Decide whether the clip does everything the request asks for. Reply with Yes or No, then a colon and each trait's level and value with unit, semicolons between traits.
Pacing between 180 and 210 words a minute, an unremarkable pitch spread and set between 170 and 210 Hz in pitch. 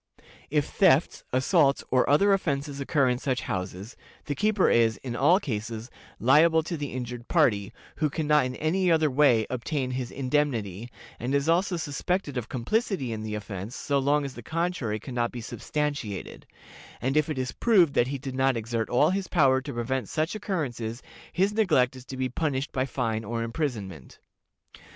No: average, 185 wpm; average, 4.6 semitones; low, 135 Hz